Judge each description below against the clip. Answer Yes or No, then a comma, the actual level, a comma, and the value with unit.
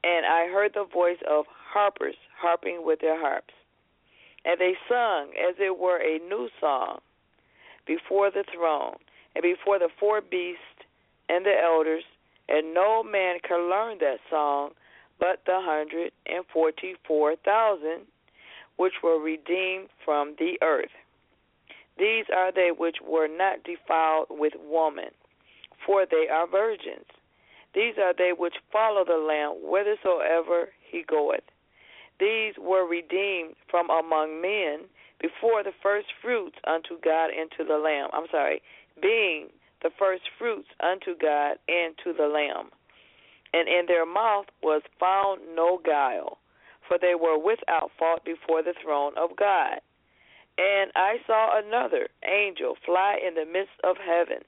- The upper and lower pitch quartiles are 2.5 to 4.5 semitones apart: Yes, average, 3.9 semitones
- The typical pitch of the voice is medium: Yes, medium, 180 Hz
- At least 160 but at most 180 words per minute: No, average, 145 wpm